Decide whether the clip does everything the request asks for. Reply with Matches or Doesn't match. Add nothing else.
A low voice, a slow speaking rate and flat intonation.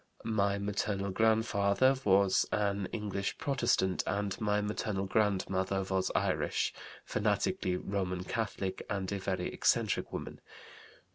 Matches